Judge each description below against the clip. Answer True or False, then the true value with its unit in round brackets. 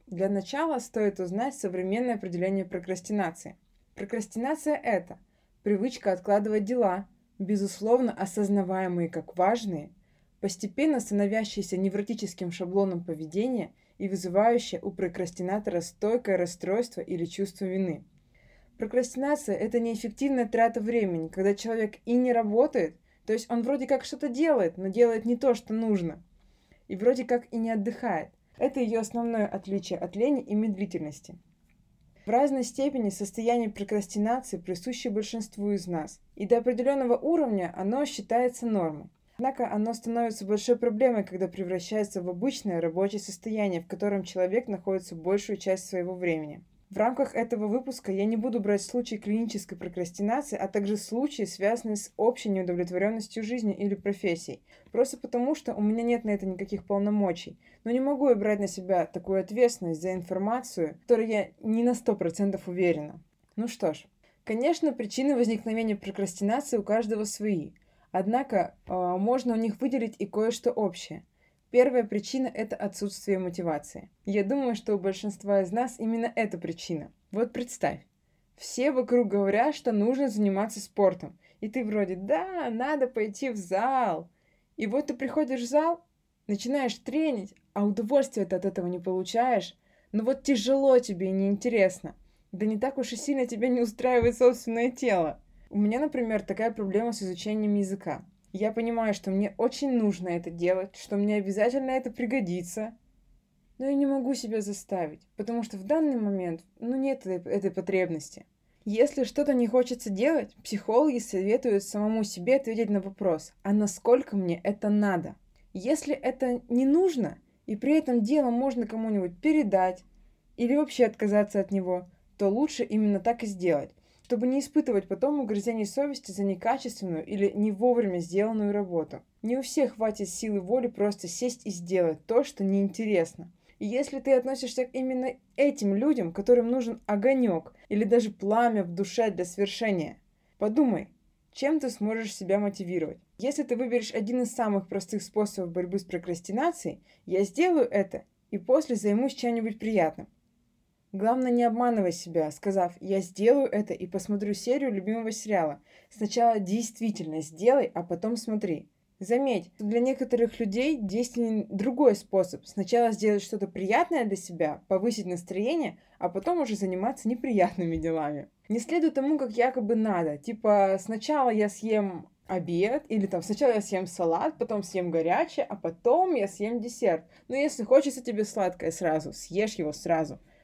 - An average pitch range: True (4.1 semitones)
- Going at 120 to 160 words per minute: True (150 wpm)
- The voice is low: False (210 Hz)